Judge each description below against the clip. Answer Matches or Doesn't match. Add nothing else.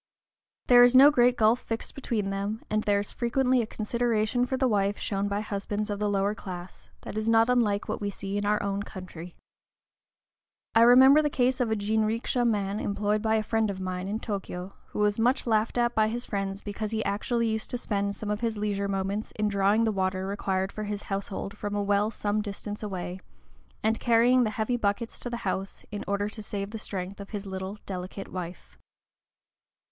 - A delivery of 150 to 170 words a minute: Doesn't match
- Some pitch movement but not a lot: Doesn't match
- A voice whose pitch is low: Doesn't match